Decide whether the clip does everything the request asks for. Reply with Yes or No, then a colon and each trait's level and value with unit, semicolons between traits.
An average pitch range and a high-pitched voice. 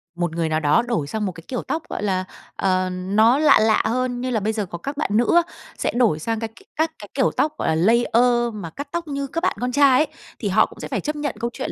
No: wide, 6.3 semitones; high, 230 Hz